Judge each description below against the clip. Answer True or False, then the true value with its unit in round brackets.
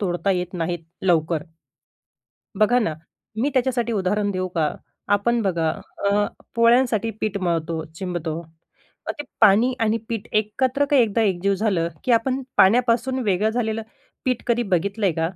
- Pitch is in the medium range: False (205 Hz)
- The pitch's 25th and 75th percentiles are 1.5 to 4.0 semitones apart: False (4.7 semitones)